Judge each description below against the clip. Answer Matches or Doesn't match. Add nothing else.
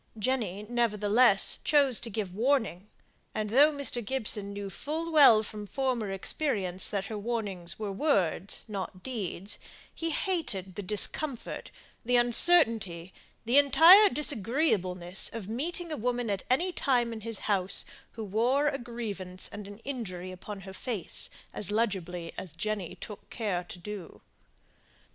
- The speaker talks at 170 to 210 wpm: Doesn't match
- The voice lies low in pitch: Doesn't match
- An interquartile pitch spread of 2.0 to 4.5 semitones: Doesn't match